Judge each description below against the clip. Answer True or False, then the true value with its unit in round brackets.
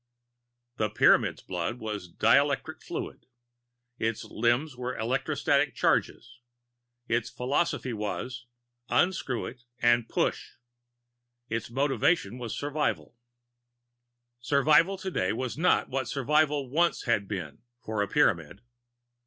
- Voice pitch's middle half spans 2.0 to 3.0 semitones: False (4.3 semitones)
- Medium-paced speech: False (105 wpm)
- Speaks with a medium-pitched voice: False (125 Hz)